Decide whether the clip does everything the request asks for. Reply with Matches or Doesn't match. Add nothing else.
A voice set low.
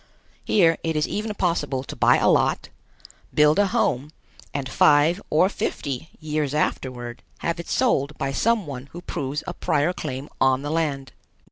Doesn't match